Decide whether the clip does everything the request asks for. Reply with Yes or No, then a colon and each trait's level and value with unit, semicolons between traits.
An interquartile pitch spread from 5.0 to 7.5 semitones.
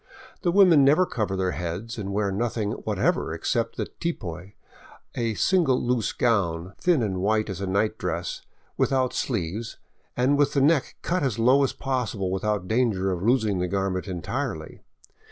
Yes: wide, 5.5 semitones